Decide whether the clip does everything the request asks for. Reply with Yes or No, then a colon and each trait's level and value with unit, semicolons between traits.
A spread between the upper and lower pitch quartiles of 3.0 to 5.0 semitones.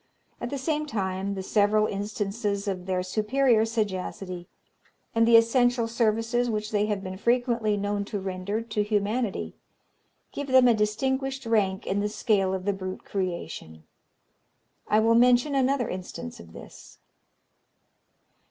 Yes: average, 3.5 semitones